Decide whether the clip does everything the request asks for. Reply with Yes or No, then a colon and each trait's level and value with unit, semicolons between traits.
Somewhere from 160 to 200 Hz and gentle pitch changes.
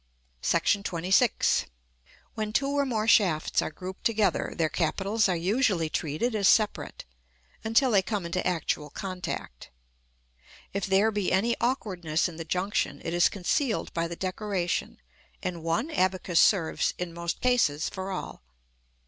No: high, 190 Hz; average, 4.1 semitones